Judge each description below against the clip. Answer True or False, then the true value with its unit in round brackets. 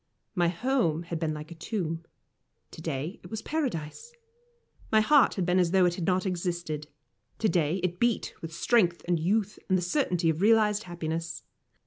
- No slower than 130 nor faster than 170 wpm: False (180 wpm)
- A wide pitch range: False (4.2 semitones)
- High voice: False (175 Hz)